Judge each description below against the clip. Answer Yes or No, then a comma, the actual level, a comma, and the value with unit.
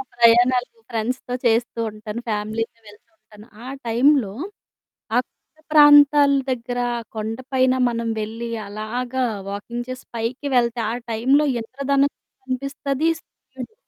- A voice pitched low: No, high, 245 Hz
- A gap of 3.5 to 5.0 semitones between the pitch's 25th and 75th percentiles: No, average, 3.0 semitones